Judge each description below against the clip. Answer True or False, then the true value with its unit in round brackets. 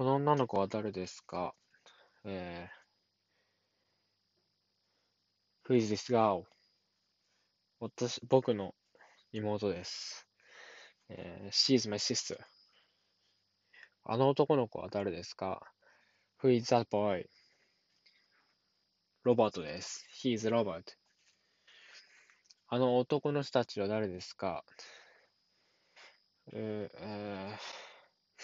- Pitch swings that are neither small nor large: True (3.9 semitones)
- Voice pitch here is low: True (105 Hz)